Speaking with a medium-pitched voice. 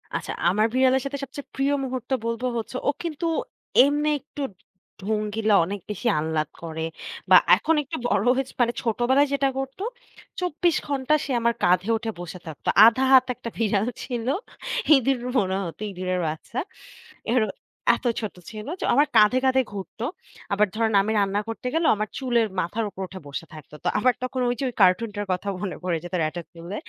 No: high, 225 Hz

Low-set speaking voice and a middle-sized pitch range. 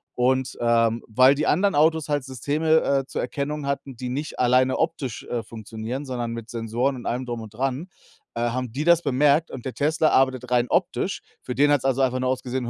Yes: low, 130 Hz; average, 3.0 semitones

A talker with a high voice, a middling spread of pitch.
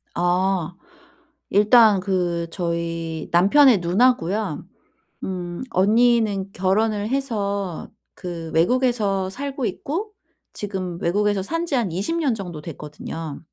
Yes: high, 195 Hz; average, 4.8 semitones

